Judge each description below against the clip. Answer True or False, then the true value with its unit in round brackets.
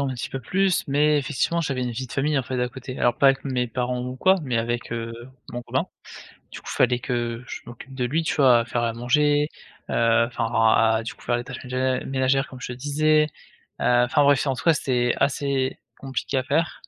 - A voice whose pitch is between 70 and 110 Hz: False (130 Hz)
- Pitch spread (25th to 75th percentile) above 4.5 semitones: False (2.5 semitones)